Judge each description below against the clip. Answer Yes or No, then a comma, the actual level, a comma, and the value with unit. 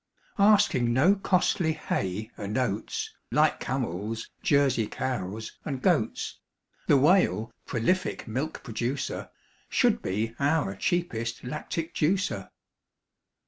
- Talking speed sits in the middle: No, slow, 100 wpm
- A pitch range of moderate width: No, wide, 6.4 semitones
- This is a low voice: Yes, low, 130 Hz